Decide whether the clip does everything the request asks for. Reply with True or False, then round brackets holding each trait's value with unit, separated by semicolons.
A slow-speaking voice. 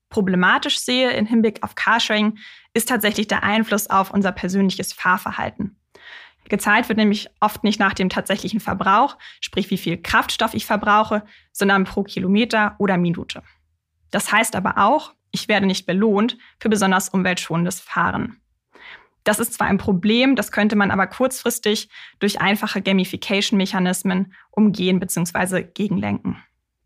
False (140 wpm)